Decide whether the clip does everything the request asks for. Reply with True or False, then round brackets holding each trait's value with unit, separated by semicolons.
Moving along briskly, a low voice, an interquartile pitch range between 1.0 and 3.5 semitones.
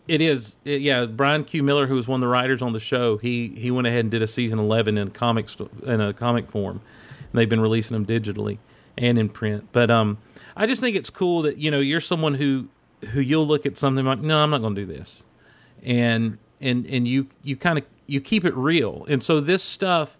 False (245 wpm; 125 Hz; 4.1 semitones)